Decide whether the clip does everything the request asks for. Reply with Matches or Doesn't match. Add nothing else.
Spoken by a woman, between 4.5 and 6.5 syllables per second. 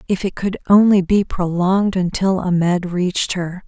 Matches